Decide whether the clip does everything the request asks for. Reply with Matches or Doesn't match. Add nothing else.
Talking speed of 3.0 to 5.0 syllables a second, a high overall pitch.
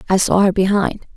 Doesn't match